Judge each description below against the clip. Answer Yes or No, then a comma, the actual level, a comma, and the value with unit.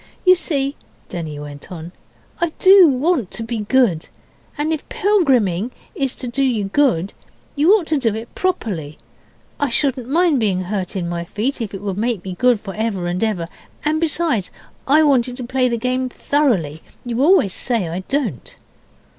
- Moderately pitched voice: No, high, 240 Hz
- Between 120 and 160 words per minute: No, average, 180 wpm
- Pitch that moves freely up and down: Yes, wide, 7.0 semitones